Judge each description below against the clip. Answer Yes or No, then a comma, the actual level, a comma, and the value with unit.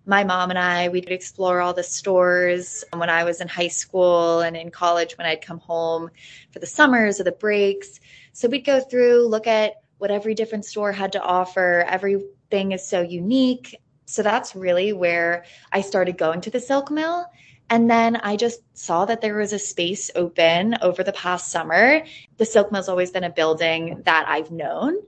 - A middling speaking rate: Yes, average, 195 wpm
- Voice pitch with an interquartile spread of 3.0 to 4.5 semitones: Yes, average, 3.9 semitones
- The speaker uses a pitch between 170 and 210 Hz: Yes, medium, 185 Hz